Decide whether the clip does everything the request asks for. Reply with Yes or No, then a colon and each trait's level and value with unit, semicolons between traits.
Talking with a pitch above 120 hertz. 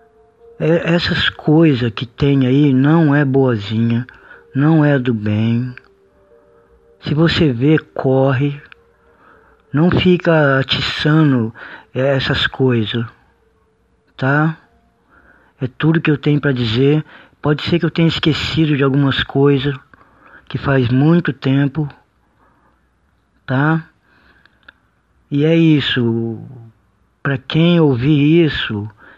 Yes: medium, 140 Hz